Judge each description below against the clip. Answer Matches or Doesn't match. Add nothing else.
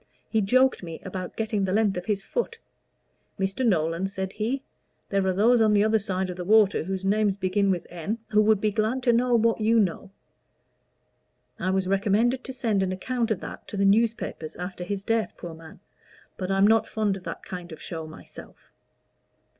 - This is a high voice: Matches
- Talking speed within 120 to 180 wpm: Doesn't match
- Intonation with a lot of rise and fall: Doesn't match